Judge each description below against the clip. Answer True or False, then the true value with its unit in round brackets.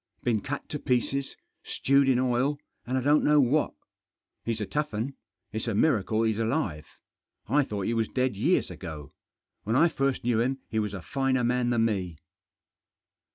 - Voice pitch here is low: True (120 Hz)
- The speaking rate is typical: True (180 wpm)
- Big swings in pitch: False (3.9 semitones)